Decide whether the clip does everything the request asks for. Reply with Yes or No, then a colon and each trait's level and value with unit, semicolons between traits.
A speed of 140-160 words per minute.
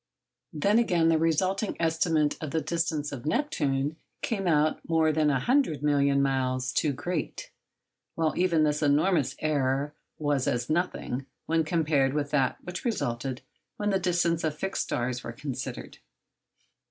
Yes: average, 155 wpm